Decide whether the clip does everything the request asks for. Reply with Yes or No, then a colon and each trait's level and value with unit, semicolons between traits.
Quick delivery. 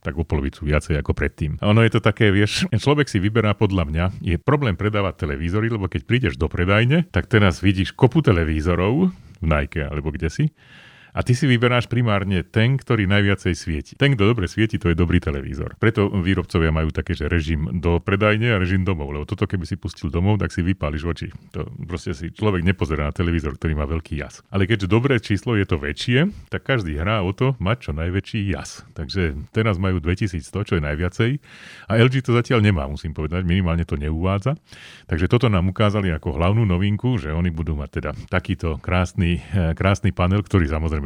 Yes: fast, 200 wpm